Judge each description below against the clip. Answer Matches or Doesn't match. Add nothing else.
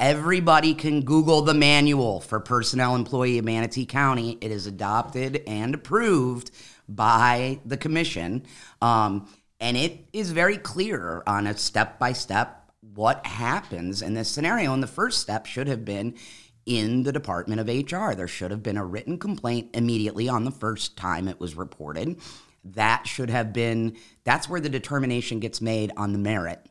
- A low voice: Matches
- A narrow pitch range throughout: Doesn't match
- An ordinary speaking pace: Matches